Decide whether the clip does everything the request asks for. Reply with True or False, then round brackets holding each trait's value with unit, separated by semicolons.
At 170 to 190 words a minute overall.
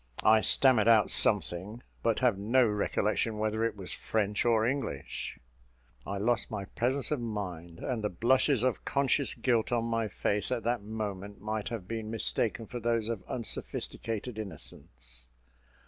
False (155 wpm)